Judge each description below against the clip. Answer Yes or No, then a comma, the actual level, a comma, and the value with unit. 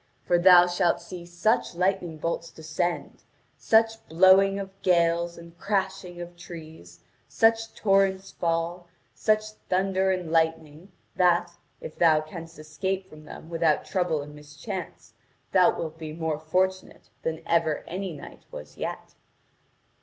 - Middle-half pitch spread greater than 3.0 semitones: No, average, 2.7 semitones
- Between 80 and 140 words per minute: Yes, slow, 135 wpm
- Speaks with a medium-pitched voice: Yes, medium, 175 Hz